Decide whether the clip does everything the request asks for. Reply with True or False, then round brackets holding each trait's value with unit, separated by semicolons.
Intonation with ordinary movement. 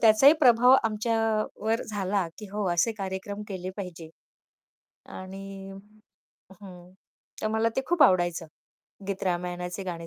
True (3.3 semitones)